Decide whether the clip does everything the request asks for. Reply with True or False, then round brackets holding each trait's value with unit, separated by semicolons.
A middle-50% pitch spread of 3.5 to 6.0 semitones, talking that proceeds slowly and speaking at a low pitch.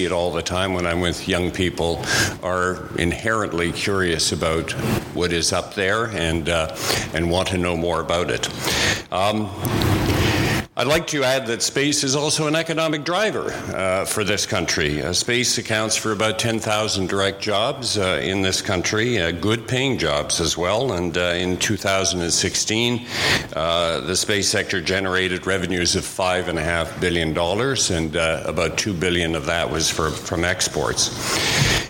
False (4.2 semitones; 160 wpm; 95 Hz)